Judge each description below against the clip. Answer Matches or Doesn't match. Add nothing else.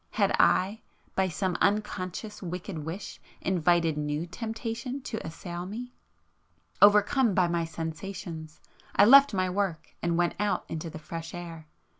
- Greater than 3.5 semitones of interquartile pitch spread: Matches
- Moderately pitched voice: Matches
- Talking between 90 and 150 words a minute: Matches